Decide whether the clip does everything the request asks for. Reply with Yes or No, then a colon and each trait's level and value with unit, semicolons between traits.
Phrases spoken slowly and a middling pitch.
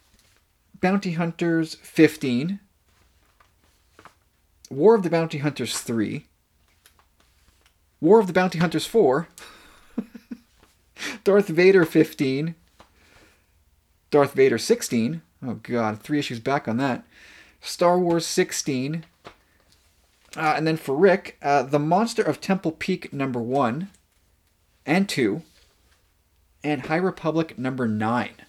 Yes: slow, 105 wpm; medium, 145 Hz